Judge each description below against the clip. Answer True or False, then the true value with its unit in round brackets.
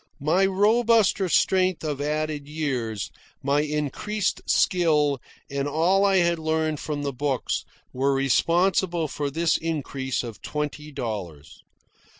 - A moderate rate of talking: False (125 wpm)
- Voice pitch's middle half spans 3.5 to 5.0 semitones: True (3.8 semitones)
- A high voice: False (150 Hz)